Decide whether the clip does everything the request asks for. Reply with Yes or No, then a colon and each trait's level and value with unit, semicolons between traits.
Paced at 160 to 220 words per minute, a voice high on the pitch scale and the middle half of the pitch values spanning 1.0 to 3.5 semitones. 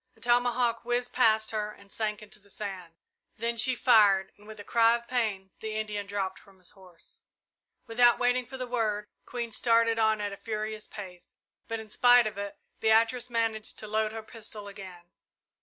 Yes: average, 190 wpm; high, 220 Hz; narrow, 2.4 semitones